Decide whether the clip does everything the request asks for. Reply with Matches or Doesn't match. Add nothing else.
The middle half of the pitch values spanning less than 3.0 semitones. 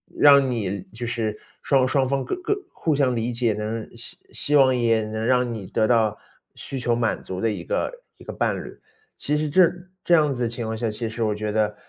Doesn't match